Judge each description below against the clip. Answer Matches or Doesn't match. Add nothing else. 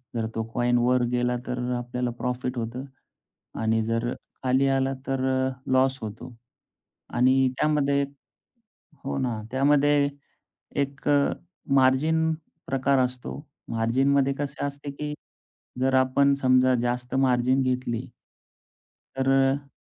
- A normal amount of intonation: Doesn't match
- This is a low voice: Matches